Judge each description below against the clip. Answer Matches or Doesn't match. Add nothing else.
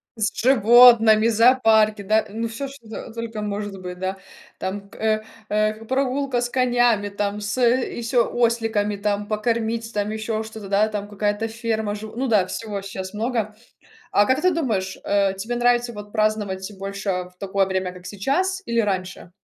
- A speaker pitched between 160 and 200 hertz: Doesn't match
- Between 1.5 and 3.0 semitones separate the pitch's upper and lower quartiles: Matches